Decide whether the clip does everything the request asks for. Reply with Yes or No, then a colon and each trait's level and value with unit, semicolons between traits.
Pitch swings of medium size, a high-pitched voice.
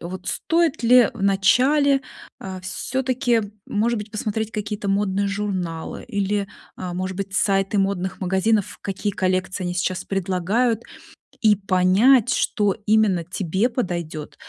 Yes: average, 3.0 semitones; high, 200 Hz